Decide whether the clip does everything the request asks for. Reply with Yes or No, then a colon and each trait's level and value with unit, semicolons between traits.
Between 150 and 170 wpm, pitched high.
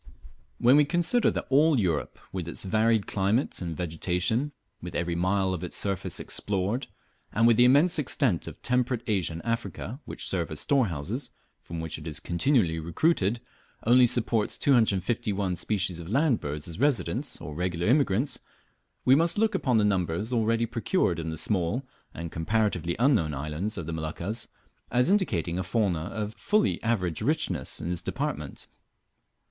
No: average, 165 wpm; low, 100 Hz